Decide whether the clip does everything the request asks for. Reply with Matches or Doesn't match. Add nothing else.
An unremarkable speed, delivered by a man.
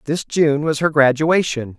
Matches